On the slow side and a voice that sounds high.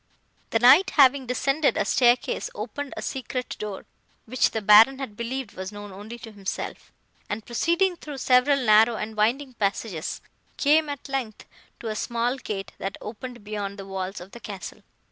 No: average, 170 wpm; high, 235 Hz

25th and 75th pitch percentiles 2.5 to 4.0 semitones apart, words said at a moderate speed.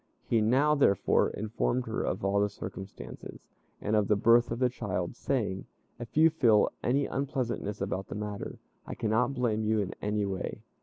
Yes: average, 3.5 semitones; average, 175 wpm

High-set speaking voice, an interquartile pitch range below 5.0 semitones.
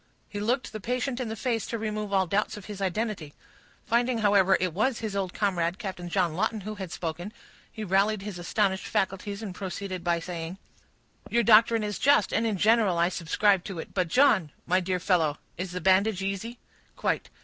Yes: high, 200 Hz; average, 3.1 semitones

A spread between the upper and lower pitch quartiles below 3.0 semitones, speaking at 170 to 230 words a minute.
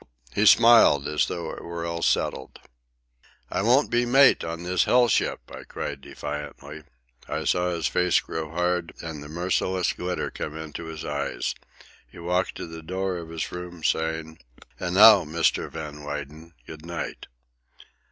No: narrow, 2.5 semitones; average, 160 wpm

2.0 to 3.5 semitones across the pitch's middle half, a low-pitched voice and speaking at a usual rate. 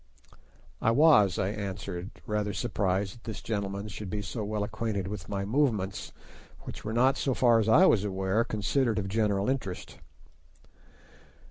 Yes: narrow, 2.6 semitones; low, 105 Hz; average, 155 wpm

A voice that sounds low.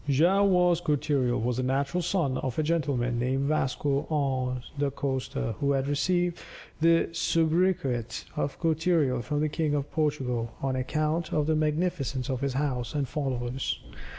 No: medium, 145 Hz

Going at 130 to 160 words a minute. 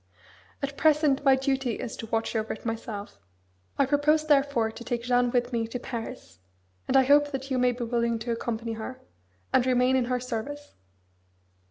No: average, 185 wpm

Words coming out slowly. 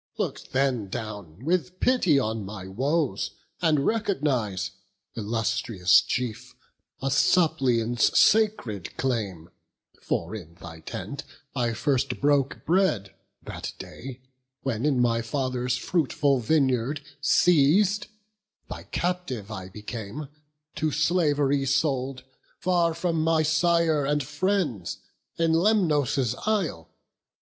Yes: slow, 105 wpm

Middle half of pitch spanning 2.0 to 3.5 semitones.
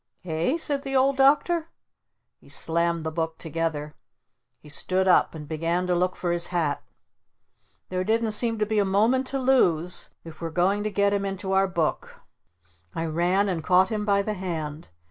No: average, 4.3 semitones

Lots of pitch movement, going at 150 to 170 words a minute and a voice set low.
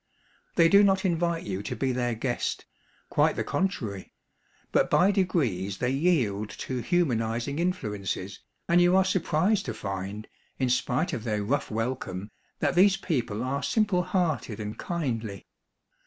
Yes: wide, 8.5 semitones; average, 155 wpm; low, 130 Hz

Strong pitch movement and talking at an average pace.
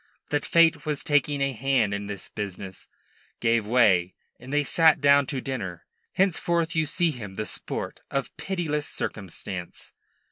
Yes: wide, 6.7 semitones; average, 150 wpm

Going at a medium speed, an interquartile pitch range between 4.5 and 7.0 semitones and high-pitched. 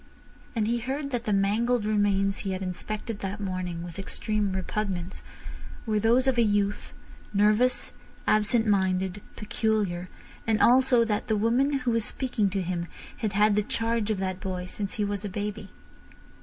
No: average, 170 wpm; average, 2.9 semitones; high, 210 Hz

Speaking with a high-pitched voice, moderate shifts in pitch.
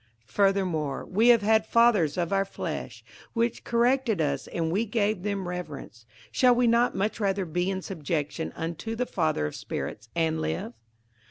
No: high, 195 Hz; wide, 5.7 semitones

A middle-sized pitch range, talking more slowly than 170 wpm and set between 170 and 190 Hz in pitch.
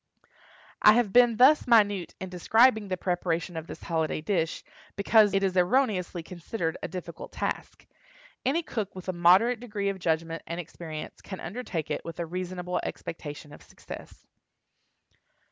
Yes: average, 4.2 semitones; average, 155 wpm; medium, 185 Hz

